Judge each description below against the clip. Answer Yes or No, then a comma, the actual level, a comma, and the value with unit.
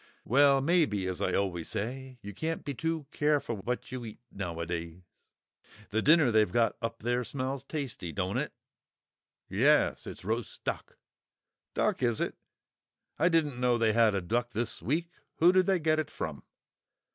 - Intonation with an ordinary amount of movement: No, wide, 5.9 semitones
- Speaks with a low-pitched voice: Yes, low, 120 Hz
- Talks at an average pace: Yes, average, 165 wpm